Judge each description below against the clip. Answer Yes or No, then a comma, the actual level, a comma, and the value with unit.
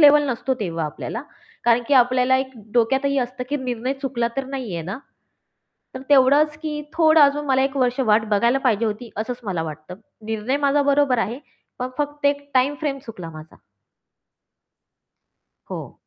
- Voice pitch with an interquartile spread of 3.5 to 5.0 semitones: Yes, average, 3.9 semitones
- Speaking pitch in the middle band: No, very high, 255 Hz